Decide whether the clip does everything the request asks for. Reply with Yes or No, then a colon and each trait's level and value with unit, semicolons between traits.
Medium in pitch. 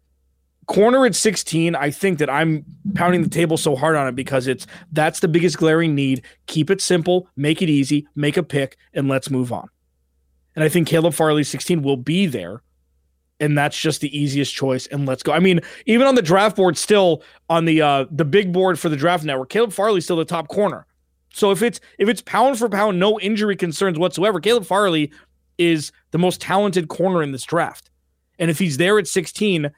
Yes: medium, 165 Hz